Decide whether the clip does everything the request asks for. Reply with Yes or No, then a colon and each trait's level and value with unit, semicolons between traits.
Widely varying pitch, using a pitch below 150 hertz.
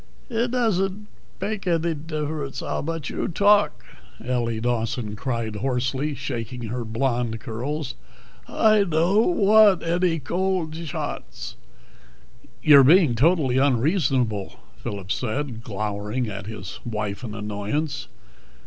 Yes: wide, 6.8 semitones; low, 135 Hz